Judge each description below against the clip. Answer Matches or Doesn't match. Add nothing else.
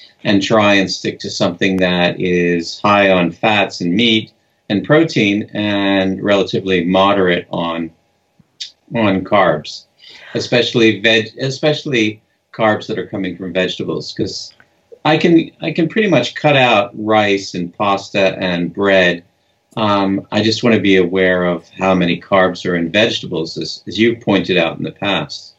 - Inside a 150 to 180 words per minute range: Matches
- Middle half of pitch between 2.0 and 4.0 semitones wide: Matches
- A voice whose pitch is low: Matches